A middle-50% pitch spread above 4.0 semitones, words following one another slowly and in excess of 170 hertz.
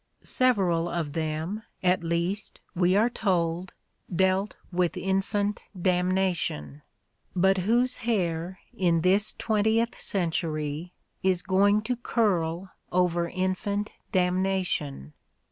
No: average, 3.0 semitones; slow, 100 wpm; medium, 185 Hz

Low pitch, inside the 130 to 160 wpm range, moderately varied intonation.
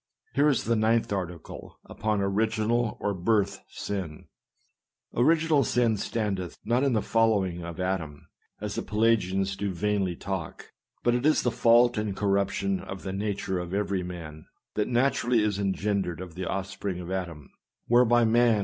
No: low, 100 Hz; average, 175 wpm; average, 3.5 semitones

